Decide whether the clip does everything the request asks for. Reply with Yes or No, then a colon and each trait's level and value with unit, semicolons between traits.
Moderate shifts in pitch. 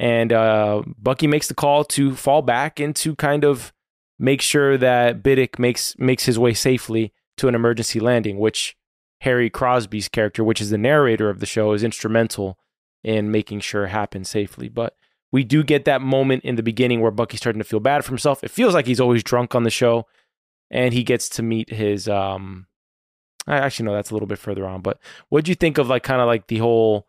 Yes: average, 3.6 semitones